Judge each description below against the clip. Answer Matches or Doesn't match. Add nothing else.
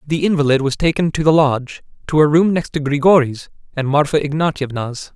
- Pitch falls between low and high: Matches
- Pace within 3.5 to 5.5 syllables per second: Doesn't match